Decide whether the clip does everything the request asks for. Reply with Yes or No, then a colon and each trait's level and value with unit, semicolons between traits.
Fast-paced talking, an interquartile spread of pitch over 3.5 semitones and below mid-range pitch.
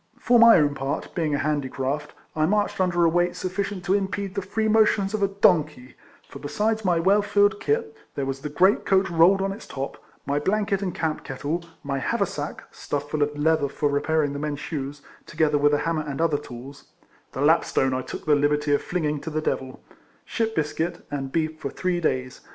No: fast, 210 wpm; average, 5.0 semitones; medium, 160 Hz